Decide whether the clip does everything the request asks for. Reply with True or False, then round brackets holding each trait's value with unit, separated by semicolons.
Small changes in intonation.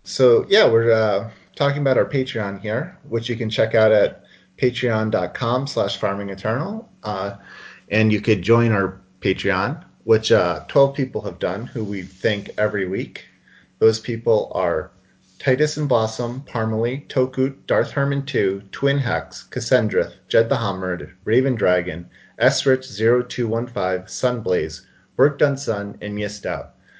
False (4.6 semitones)